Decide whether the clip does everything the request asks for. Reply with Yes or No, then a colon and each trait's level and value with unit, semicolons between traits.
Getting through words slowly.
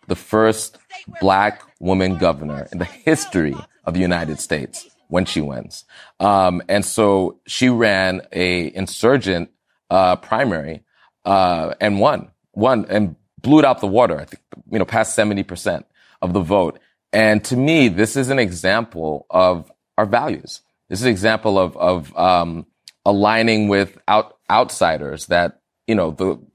No: average, 155 wpm